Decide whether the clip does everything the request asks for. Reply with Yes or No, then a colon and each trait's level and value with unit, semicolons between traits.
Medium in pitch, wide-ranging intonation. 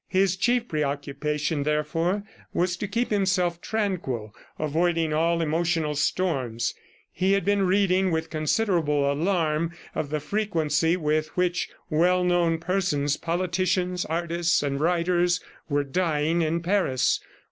No: medium, 170 Hz; average, 3.2 semitones